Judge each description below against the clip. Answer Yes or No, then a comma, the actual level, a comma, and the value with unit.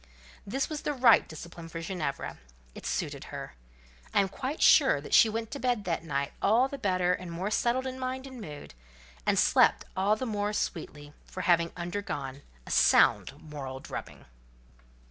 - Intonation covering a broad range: Yes, wide, 6.8 semitones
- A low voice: No, high, 195 Hz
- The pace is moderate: Yes, average, 170 wpm